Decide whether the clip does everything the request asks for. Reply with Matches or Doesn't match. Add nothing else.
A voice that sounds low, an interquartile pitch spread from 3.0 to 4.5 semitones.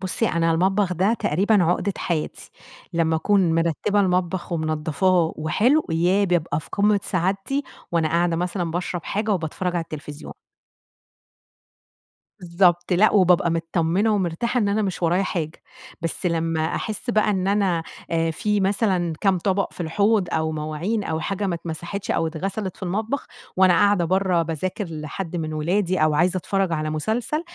Doesn't match